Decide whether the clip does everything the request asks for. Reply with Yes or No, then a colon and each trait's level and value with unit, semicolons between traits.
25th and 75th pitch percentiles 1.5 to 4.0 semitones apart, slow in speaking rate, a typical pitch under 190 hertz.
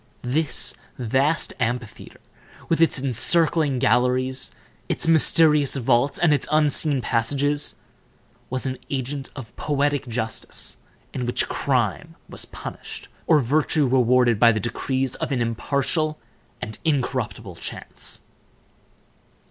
Yes: average, 3.2 semitones; slow, 115 wpm; low, 135 Hz